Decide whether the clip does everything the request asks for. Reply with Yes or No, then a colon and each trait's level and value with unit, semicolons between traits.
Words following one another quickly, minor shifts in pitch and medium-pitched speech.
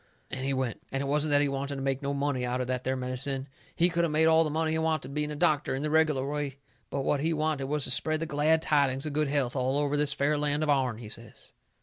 Yes: fast, 280 wpm; narrow, 2.3 semitones; medium, 145 Hz